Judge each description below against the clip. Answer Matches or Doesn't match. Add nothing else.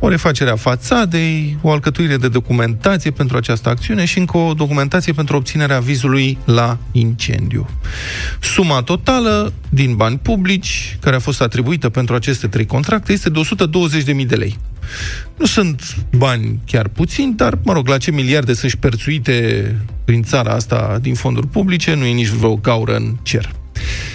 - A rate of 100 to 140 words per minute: Doesn't match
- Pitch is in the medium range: Doesn't match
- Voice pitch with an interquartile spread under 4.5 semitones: Doesn't match